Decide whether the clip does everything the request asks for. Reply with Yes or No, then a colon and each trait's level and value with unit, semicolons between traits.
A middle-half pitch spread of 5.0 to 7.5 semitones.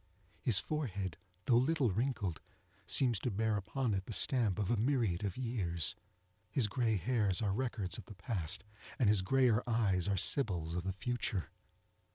No: average, 4.6 semitones